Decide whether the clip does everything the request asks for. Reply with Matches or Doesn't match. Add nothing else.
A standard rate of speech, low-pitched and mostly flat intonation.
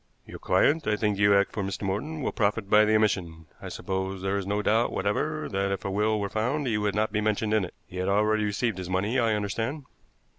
Doesn't match